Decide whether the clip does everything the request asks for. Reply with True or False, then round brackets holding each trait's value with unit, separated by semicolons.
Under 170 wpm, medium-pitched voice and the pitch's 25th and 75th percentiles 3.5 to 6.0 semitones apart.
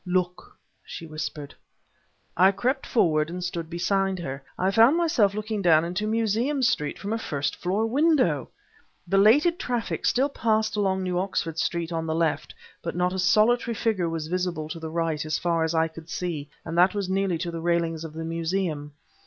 False (185 wpm; 180 Hz; 4.6 semitones)